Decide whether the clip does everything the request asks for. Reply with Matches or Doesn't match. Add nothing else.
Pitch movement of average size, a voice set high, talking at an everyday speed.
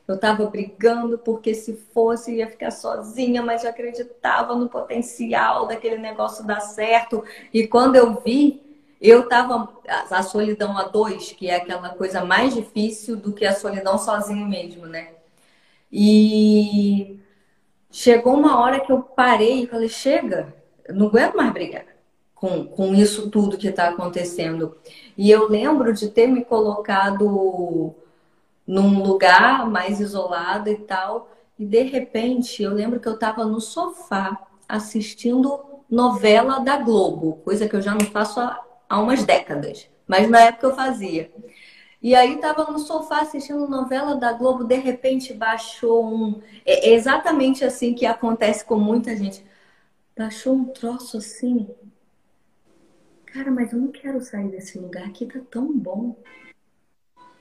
Matches